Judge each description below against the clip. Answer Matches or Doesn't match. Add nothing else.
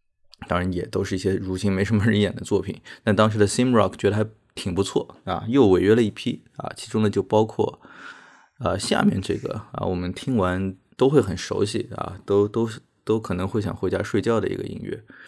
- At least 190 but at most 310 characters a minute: Doesn't match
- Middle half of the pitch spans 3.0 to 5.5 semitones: Doesn't match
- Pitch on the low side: Matches